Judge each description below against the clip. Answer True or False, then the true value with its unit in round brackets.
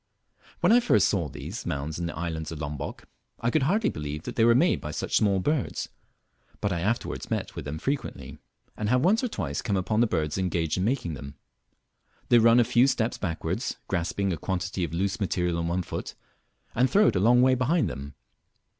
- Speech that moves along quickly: True (210 wpm)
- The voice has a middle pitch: False (95 Hz)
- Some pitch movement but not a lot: False (6.8 semitones)